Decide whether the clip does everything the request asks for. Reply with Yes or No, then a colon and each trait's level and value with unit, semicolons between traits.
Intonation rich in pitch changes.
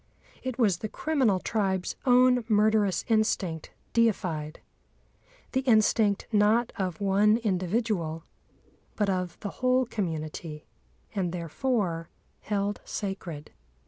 No: average, 4.2 semitones